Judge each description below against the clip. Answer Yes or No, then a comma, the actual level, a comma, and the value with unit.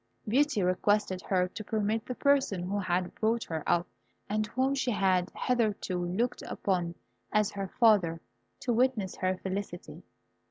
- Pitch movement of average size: Yes, average, 3.9 semitones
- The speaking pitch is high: Yes, high, 205 Hz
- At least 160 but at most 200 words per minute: No, average, 150 wpm